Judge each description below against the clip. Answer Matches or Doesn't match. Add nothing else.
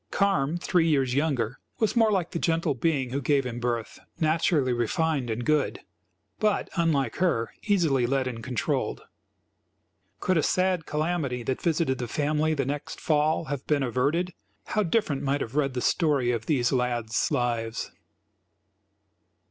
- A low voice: Doesn't match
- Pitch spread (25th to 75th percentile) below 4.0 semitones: Doesn't match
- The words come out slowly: Doesn't match